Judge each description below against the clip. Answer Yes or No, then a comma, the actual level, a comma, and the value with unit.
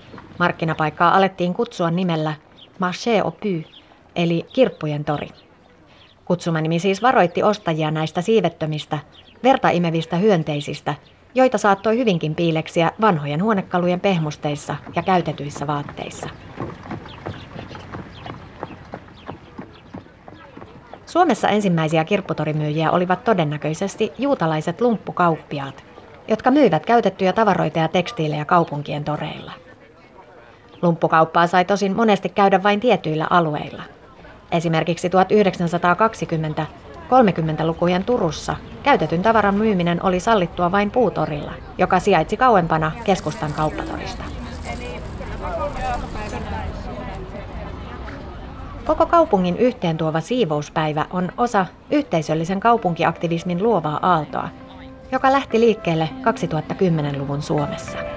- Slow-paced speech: Yes, slow, 85 wpm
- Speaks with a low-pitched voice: No, medium, 175 Hz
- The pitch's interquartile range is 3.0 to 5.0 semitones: Yes, average, 4.6 semitones